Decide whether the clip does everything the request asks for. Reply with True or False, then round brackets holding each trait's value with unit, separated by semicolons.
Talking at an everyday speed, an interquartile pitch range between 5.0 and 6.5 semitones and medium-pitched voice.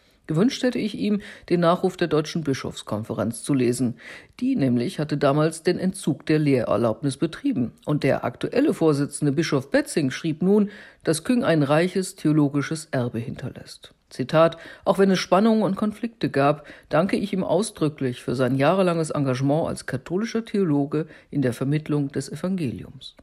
True (150 wpm; 5.4 semitones; 155 Hz)